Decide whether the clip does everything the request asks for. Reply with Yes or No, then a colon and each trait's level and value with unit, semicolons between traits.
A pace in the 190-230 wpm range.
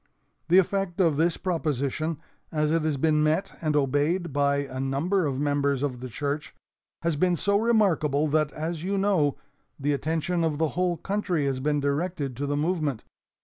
No: average, 180 wpm